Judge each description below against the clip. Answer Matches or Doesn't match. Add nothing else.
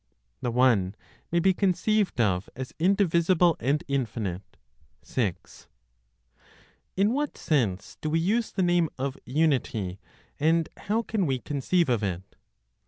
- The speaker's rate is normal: Doesn't match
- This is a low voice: Doesn't match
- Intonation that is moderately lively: Doesn't match